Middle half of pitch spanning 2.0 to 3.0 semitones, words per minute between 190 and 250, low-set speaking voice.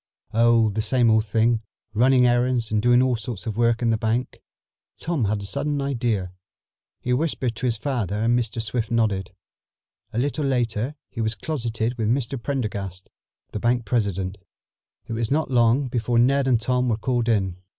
No: narrow, 2.5 semitones; average, 180 wpm; low, 115 Hz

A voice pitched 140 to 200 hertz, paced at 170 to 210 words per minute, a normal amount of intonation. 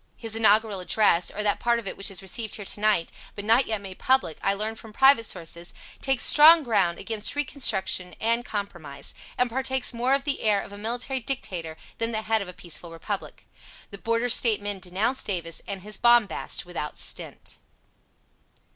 No: high, 215 Hz; average, 190 wpm; average, 3.8 semitones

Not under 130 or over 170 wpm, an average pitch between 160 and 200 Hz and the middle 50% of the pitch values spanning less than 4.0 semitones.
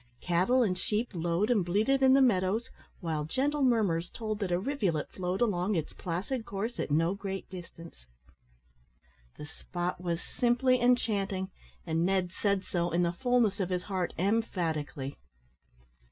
No: average, 155 wpm; high, 190 Hz; average, 4.7 semitones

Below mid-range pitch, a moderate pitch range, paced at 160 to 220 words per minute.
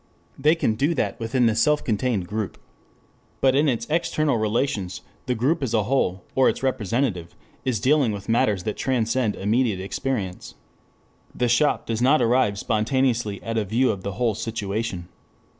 Yes: low, 115 Hz; average, 3.9 semitones; average, 165 wpm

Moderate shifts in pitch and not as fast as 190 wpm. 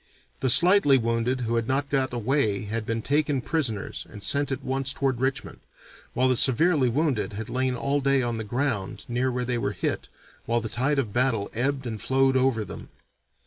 No: average, 3.0 semitones; average, 195 wpm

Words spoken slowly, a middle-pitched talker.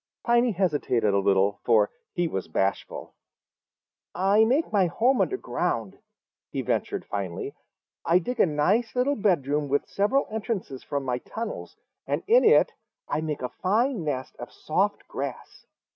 No: average, 150 wpm; medium, 180 Hz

